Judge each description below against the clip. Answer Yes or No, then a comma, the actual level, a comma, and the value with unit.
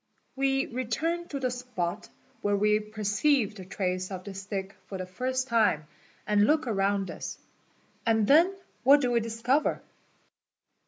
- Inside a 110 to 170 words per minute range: Yes, average, 150 wpm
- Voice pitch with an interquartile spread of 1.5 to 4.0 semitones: No, average, 4.8 semitones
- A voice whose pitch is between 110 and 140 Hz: No, high, 220 Hz